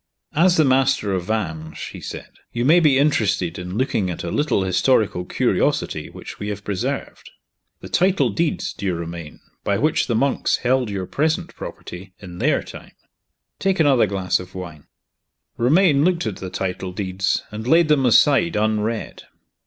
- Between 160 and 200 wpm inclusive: Yes, average, 165 wpm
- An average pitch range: No, wide, 7.6 semitones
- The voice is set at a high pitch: No, low, 110 Hz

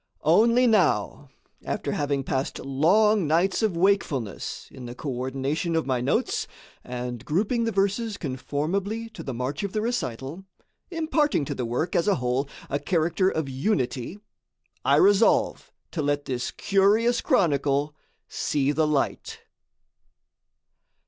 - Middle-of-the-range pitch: Yes, medium, 155 Hz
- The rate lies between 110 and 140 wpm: Yes, slow, 135 wpm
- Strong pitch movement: Yes, wide, 7.0 semitones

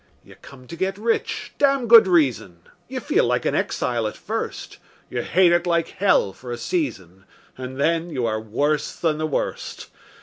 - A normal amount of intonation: No, wide, 7.1 semitones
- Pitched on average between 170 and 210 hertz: No, medium, 155 Hz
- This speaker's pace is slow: No, average, 180 wpm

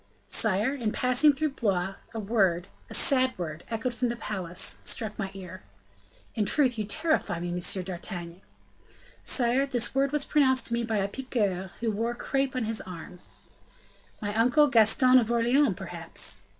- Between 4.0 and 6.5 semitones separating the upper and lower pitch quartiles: Yes, average, 5.0 semitones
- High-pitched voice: Yes, high, 225 Hz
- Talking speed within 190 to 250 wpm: No, average, 165 wpm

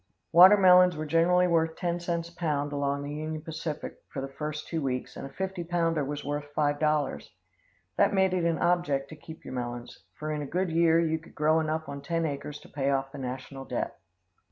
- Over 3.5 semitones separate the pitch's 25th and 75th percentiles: No, average, 2.9 semitones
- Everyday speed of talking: No, fast, 210 wpm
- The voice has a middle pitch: Yes, medium, 155 Hz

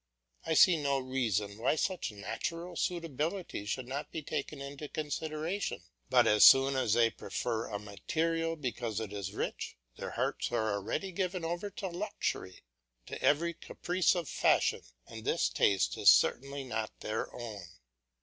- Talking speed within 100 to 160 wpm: Yes, average, 155 wpm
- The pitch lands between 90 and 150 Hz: Yes, medium, 140 Hz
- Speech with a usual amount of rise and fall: No, wide, 7.1 semitones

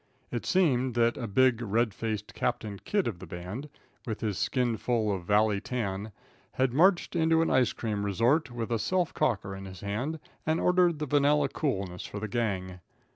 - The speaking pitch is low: Yes, low, 115 Hz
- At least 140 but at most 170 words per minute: No, average, 185 wpm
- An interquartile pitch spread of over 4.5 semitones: Yes, wide, 5.6 semitones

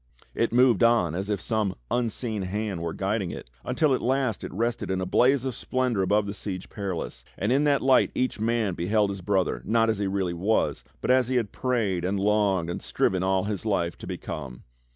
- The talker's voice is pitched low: Yes, low, 105 Hz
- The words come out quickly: Yes, fast, 215 wpm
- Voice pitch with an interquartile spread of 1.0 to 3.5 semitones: No, average, 3.9 semitones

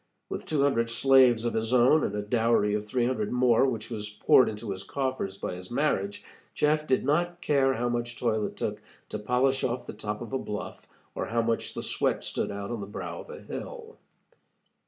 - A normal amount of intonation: Yes, average, 4.0 semitones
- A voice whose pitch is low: Yes, low, 120 Hz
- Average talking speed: No, fast, 215 wpm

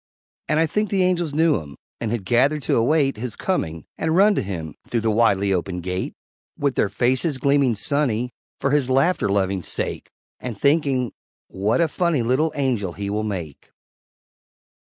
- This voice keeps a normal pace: Yes, average, 170 wpm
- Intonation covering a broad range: Yes, wide, 6.9 semitones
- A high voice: No, low, 125 Hz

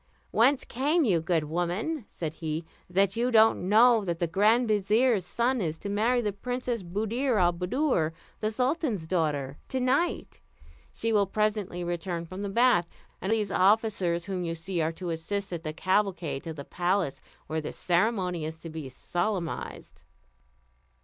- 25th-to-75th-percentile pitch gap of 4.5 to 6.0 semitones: Yes, average, 4.8 semitones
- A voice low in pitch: No, high, 190 Hz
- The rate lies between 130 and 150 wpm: No, average, 165 wpm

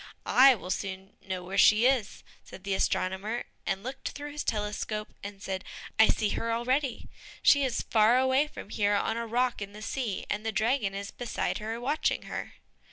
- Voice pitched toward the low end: No, high, 220 Hz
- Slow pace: No, average, 190 wpm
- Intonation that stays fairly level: No, average, 3.9 semitones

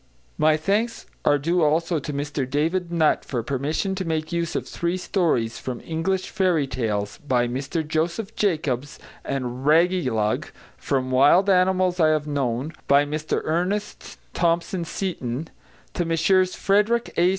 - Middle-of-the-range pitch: Yes, medium, 160 Hz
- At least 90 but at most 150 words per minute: Yes, average, 145 wpm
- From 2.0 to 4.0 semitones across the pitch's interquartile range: No, average, 4.5 semitones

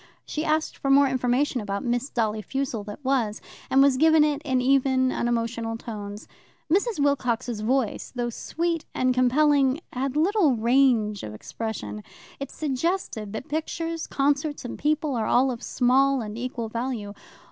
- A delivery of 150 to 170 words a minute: Yes, average, 155 wpm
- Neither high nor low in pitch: No, very high, 255 Hz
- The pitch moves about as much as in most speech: Yes, average, 3.7 semitones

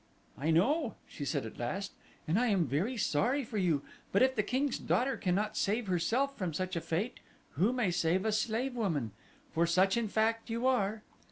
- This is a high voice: Yes, high, 210 Hz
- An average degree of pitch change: No, wide, 5.7 semitones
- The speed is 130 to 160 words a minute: No, average, 195 wpm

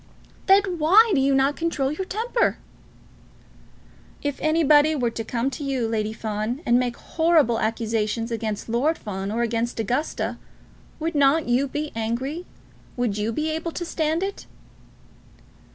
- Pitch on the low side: No, very high, 270 Hz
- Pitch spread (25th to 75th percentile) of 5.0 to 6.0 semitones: Yes, wide, 5.6 semitones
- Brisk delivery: No, average, 150 wpm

